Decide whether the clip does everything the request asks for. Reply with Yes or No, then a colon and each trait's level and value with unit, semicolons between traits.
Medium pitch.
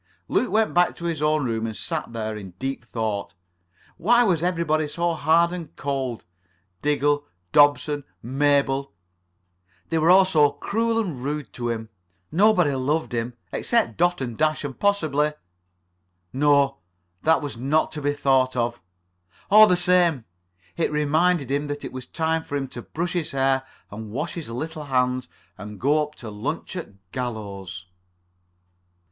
Yes: medium, 145 Hz